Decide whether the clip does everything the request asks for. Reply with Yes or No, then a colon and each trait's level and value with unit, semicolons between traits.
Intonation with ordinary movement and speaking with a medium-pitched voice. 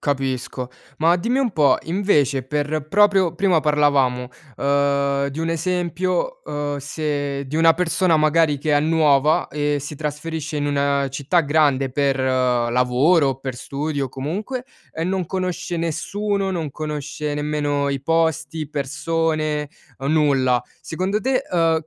Yes: average, 3.0 semitones; medium, 150 Hz